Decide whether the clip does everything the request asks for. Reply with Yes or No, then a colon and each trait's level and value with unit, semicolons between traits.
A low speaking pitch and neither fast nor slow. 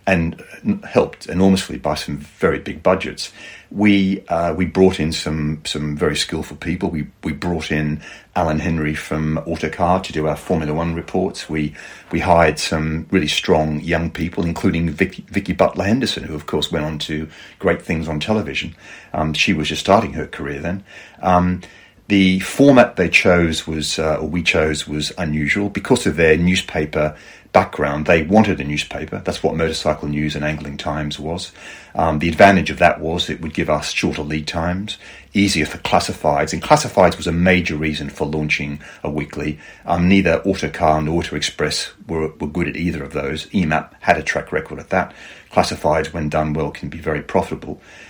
Yes: very low, 80 Hz; average, 180 wpm